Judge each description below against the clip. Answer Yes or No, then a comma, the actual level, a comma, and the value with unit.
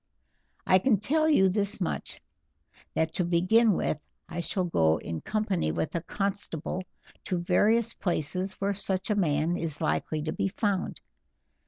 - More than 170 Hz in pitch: Yes, medium, 185 Hz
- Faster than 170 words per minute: No, average, 155 wpm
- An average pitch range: Yes, average, 3.8 semitones